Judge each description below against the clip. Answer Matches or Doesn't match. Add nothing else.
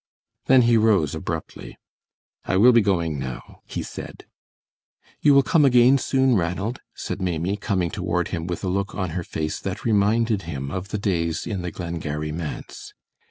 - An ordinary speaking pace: Matches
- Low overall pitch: Matches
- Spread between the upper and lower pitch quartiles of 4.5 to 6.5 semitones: Matches